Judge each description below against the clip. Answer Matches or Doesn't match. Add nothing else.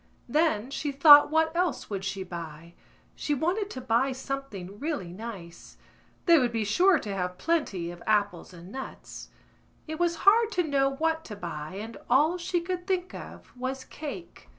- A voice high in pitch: Matches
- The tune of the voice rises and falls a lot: Matches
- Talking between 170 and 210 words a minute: Matches